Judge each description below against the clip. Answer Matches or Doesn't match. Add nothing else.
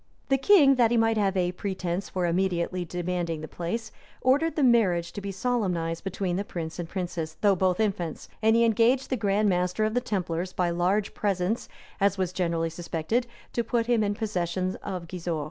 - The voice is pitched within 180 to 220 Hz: Matches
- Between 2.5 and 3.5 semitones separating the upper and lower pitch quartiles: Doesn't match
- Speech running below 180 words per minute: Doesn't match